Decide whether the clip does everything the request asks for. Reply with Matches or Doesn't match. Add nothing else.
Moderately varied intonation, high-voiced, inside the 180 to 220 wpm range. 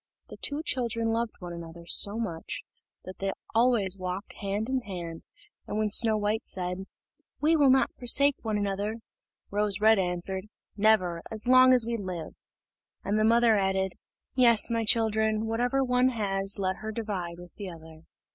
Doesn't match